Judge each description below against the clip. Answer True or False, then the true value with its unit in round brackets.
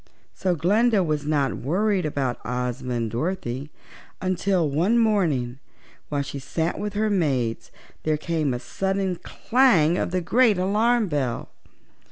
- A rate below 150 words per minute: True (140 wpm)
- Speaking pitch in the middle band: True (165 Hz)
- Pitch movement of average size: False (6.2 semitones)